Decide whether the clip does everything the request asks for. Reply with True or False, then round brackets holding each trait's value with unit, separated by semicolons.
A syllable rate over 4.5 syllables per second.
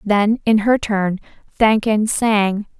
False (3.5 syllables/s)